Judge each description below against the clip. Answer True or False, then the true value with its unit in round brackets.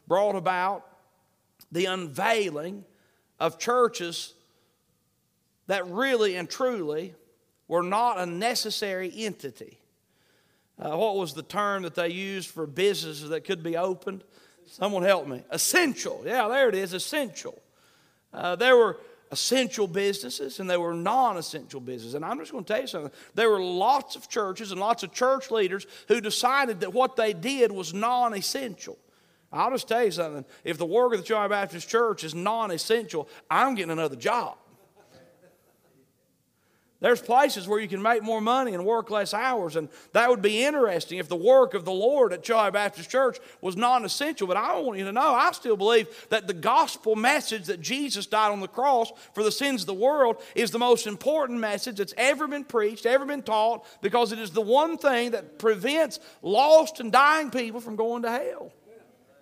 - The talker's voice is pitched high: True (215 Hz)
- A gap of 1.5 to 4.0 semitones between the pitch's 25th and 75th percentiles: False (5.0 semitones)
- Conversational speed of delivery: True (180 wpm)